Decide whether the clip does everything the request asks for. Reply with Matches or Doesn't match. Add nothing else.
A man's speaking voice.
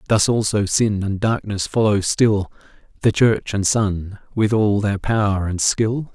Matches